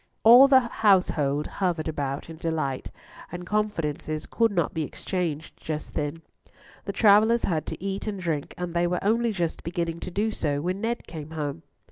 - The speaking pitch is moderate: Yes, medium, 170 Hz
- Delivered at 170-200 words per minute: Yes, average, 175 wpm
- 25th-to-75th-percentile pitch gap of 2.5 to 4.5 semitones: No, average, 4.9 semitones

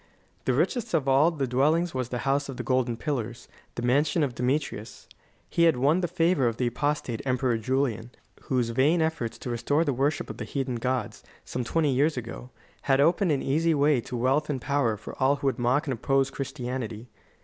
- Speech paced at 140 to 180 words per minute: No, fast, 205 wpm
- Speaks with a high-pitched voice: No, low, 135 Hz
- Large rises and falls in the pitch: No, average, 3.3 semitones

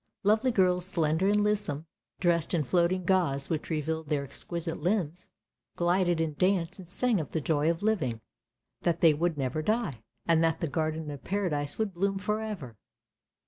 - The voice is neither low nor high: Yes, medium, 170 Hz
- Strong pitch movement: No, average, 3.7 semitones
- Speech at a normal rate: Yes, average, 185 wpm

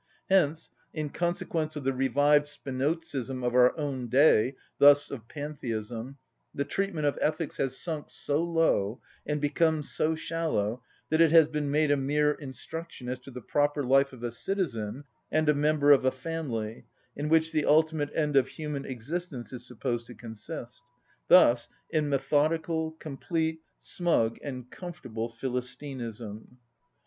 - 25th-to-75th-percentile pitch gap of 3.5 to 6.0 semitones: Yes, average, 3.9 semitones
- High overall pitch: No, medium, 145 Hz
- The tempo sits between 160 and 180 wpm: No, average, 150 wpm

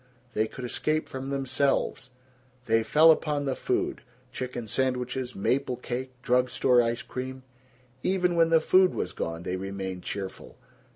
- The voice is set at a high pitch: No, low, 130 Hz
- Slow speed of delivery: No, average, 150 wpm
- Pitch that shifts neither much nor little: Yes, average, 4.0 semitones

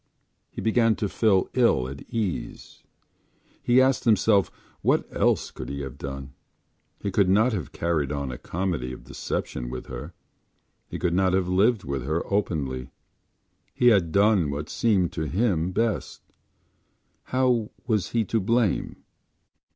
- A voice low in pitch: Yes, very low, 95 Hz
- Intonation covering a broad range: Yes, wide, 7.6 semitones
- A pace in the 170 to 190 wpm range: No, average, 150 wpm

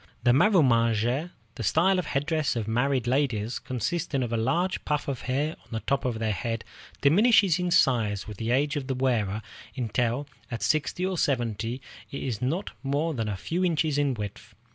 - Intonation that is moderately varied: Yes, average, 5.0 semitones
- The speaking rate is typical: Yes, average, 185 wpm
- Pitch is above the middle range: No, low, 130 Hz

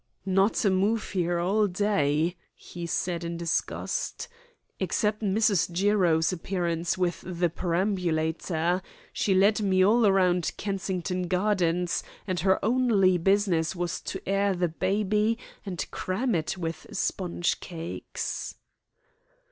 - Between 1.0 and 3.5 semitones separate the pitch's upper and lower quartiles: Yes, average, 2.7 semitones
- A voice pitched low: No, medium, 185 Hz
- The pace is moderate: No, slow, 120 wpm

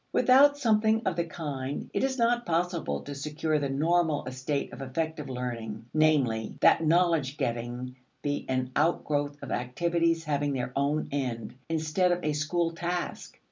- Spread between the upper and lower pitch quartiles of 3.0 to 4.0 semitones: No, average, 4.4 semitones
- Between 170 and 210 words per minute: No, average, 155 wpm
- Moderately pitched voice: Yes, medium, 155 Hz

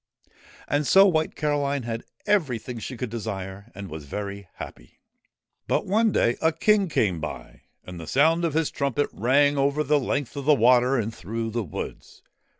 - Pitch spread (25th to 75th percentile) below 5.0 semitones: No, wide, 5.5 semitones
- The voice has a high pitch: No, low, 130 Hz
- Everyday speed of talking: Yes, average, 175 wpm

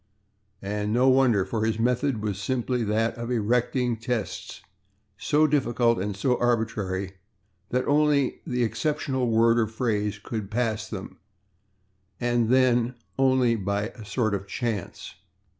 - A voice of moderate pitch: No, low, 115 Hz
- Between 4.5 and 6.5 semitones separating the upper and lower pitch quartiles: No, average, 3.0 semitones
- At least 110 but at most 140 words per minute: Yes, slow, 135 wpm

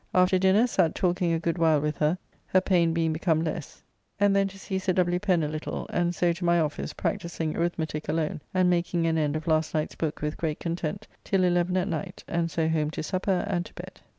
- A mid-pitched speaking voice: Yes, medium, 170 Hz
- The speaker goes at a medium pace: No, fast, 230 wpm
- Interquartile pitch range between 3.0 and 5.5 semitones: No, narrow, 2.4 semitones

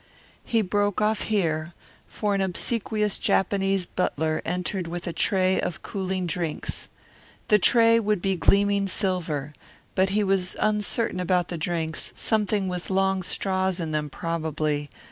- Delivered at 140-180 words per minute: Yes, average, 145 wpm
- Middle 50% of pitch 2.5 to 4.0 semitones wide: Yes, average, 3.0 semitones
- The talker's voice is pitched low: No, high, 190 Hz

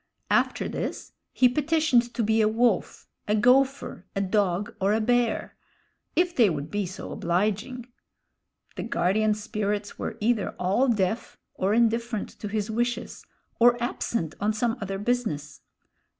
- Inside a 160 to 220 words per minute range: No, average, 145 wpm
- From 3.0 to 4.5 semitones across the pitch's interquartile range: Yes, average, 3.3 semitones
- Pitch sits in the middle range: No, high, 215 Hz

